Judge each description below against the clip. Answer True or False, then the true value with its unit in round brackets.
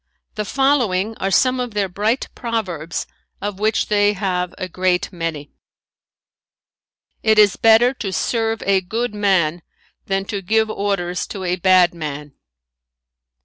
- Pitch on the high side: True (200 Hz)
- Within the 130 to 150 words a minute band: True (140 wpm)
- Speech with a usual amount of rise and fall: True (3.5 semitones)